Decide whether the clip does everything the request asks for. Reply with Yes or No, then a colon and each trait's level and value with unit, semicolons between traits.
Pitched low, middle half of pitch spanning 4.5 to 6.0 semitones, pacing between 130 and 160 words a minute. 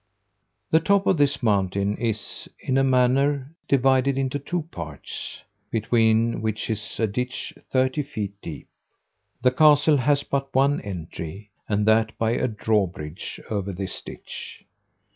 Yes: low, 115 Hz; average, 4.9 semitones; average, 140 wpm